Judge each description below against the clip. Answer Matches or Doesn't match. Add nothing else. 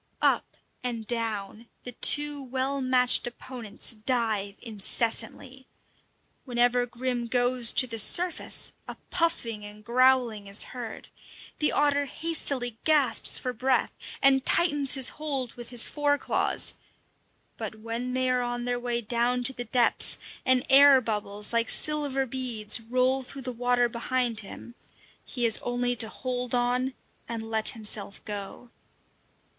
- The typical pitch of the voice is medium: Doesn't match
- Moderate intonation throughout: Doesn't match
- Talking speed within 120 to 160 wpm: Matches